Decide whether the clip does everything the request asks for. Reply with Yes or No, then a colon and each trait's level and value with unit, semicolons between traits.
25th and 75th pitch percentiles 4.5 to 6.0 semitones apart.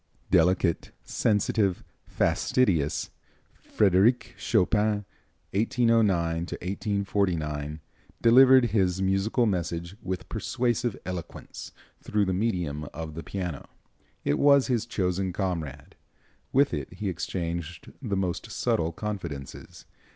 No: average, 4.1 semitones